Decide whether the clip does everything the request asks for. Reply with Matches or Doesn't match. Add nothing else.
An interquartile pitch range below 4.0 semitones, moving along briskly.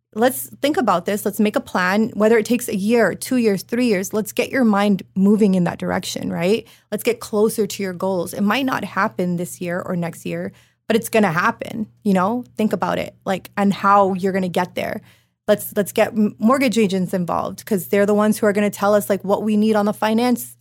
Matches